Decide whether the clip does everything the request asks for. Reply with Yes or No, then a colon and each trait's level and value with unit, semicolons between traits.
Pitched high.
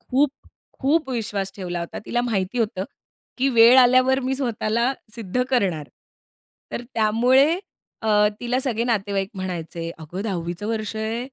Yes: high, 225 Hz